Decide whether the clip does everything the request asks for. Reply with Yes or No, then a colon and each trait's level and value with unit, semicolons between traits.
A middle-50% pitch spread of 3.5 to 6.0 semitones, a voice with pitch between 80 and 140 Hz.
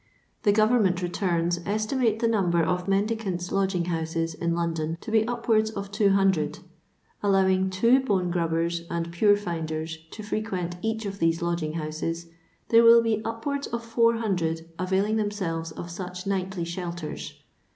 No: average, 4.2 semitones; high, 190 Hz